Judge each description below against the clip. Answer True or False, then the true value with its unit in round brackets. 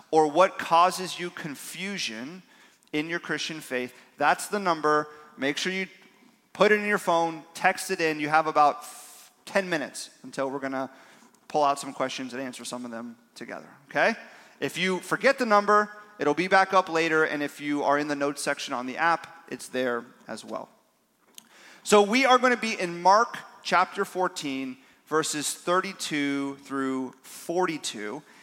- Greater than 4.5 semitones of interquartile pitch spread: True (4.9 semitones)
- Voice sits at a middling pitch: True (160 Hz)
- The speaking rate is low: False (170 wpm)